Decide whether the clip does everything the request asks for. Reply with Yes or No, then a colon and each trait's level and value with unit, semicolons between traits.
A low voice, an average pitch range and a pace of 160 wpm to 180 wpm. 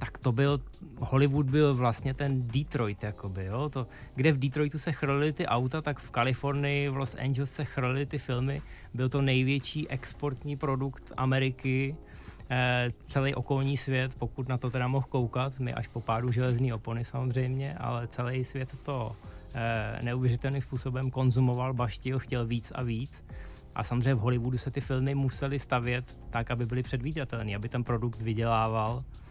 No: low, 130 Hz; narrow, 2.3 semitones; average, 165 wpm